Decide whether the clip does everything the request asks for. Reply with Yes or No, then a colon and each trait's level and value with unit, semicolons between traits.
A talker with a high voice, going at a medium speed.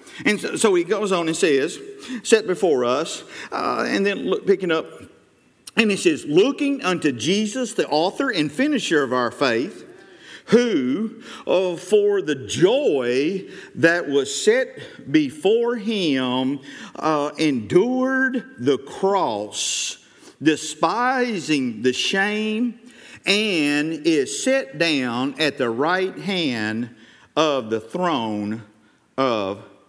No: high, 200 Hz; slow, 115 wpm